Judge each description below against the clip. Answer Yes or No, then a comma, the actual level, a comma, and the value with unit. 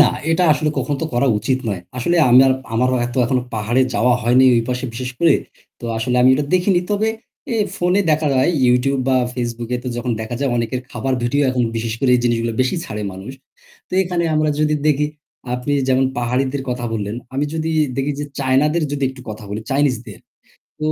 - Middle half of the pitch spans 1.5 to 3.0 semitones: No, average, 3.4 semitones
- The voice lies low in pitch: Yes, low, 130 Hz